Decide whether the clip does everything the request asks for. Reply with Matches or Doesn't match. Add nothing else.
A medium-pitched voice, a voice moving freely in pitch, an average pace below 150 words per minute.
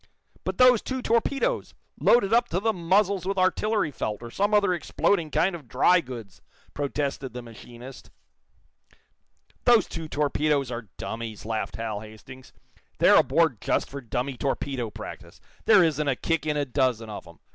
Doesn't match